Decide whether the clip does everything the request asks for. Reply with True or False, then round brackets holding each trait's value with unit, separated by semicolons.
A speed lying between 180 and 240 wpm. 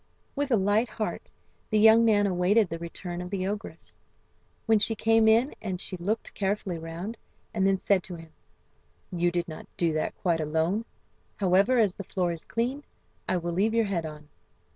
True (185 wpm)